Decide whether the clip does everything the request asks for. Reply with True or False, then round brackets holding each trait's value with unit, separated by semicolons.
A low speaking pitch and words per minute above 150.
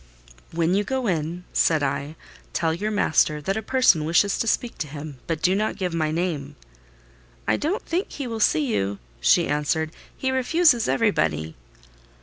False (175 Hz; 170 wpm)